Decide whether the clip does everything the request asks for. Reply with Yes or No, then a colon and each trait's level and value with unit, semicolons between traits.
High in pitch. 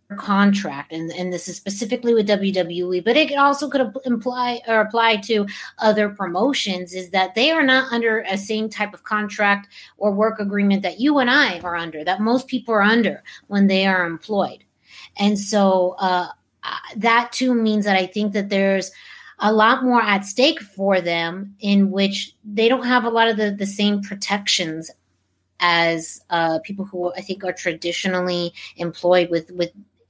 Yes: high, 200 Hz